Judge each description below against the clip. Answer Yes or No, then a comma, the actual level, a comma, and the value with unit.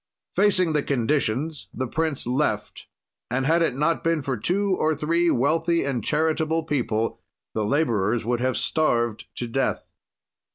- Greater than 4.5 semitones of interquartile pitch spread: Yes, average, 5.0 semitones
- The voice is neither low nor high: Yes, medium, 145 Hz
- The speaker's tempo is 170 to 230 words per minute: No, average, 150 wpm